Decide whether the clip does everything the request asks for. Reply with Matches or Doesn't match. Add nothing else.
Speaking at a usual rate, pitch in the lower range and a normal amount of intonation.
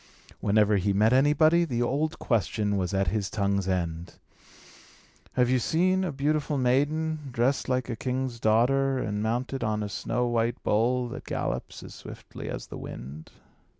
Matches